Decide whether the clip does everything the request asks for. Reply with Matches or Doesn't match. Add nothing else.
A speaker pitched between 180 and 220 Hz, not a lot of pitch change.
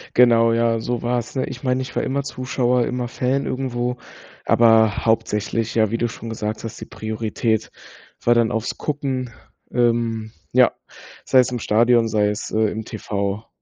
Doesn't match